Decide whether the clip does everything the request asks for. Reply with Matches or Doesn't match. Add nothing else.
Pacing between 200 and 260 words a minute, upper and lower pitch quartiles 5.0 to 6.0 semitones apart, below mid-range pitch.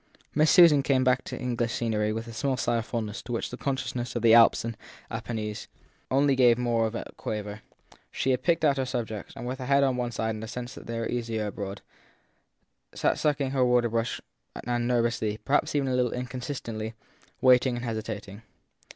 Doesn't match